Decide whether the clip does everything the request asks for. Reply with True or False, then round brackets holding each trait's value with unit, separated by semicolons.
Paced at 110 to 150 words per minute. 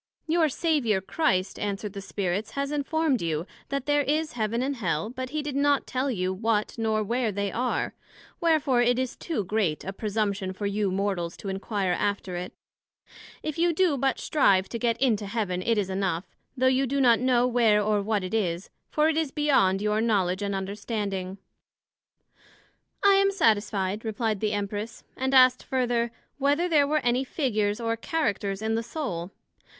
False (180 wpm)